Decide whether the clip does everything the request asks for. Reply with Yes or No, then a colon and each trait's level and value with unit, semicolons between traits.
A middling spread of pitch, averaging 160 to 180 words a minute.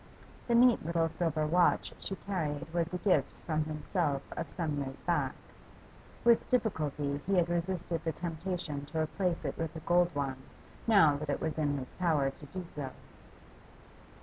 Yes: average, 3.3 semitones; average, 170 wpm